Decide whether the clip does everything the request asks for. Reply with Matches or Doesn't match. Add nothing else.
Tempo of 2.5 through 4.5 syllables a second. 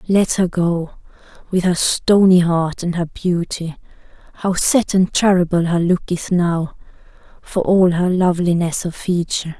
Matches